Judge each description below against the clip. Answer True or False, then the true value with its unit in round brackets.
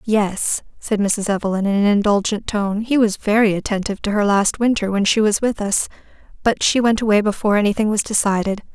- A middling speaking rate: True (190 wpm)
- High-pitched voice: True (210 Hz)